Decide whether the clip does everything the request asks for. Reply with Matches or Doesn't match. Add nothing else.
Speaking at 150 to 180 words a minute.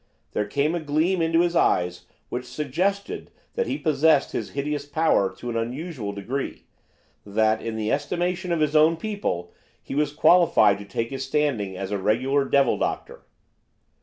Matches